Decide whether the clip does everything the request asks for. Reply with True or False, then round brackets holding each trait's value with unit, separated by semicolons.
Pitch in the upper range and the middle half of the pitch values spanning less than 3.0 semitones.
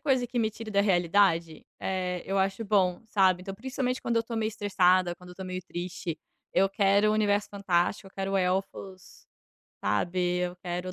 True (195 Hz; 2.5 semitones)